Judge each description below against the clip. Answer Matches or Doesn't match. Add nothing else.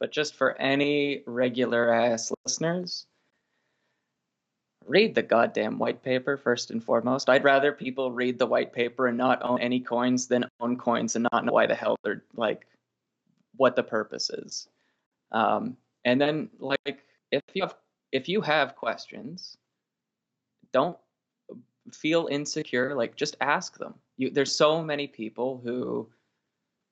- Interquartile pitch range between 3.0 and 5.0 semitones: Doesn't match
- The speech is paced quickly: Doesn't match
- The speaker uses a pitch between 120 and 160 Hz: Matches